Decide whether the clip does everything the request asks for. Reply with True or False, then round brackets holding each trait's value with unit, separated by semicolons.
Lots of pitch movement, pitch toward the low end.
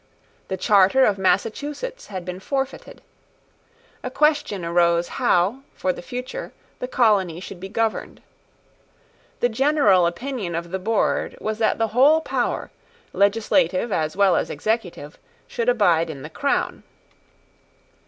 False (5.7 semitones; 210 Hz)